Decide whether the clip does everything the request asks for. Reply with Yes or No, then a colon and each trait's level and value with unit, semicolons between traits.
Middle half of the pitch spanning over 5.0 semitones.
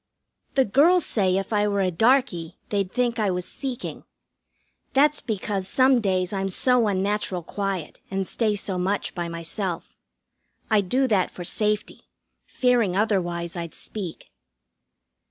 No: average, 4.0 semitones